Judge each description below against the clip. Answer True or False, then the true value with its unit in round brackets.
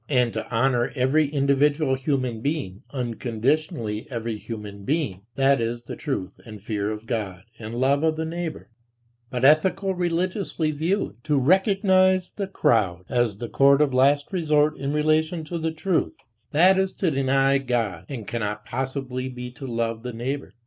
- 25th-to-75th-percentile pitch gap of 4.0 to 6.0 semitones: True (5.0 semitones)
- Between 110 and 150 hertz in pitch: True (135 Hz)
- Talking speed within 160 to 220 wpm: True (165 wpm)